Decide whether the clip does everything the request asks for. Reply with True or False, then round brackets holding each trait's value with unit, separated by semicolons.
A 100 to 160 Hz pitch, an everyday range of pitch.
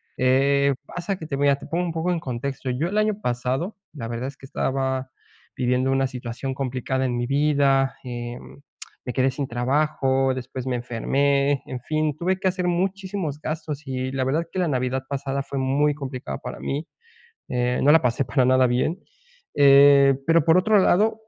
True (135 Hz; 3.1 semitones)